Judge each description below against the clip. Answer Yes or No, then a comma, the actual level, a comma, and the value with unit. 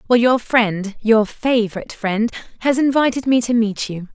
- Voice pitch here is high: Yes, high, 230 Hz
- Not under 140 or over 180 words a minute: Yes, average, 175 wpm